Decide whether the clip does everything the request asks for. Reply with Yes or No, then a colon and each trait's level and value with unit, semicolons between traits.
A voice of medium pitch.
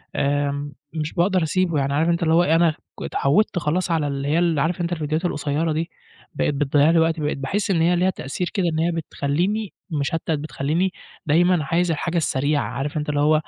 Yes: medium, 160 Hz